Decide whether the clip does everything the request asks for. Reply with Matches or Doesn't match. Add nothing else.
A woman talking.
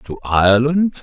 Doesn't match